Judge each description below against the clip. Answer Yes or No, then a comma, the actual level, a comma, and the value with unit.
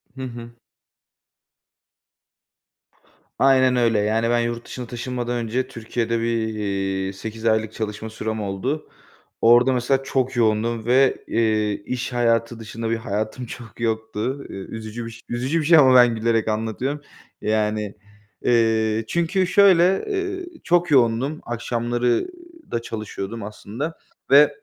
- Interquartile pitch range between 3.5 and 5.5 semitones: No, average, 2.7 semitones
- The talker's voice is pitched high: No, low, 115 Hz